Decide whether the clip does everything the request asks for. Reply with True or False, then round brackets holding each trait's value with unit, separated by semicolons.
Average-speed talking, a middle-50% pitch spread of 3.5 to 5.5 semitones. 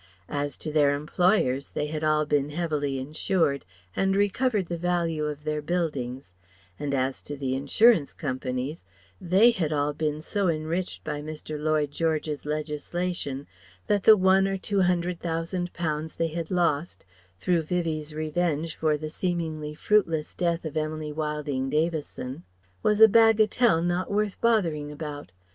False (150 wpm; 3.1 semitones)